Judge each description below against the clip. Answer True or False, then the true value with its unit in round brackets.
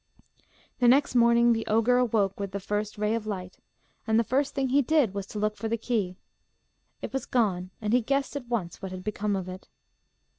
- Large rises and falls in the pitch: False (3.6 semitones)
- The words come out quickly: True (215 wpm)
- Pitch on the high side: True (220 Hz)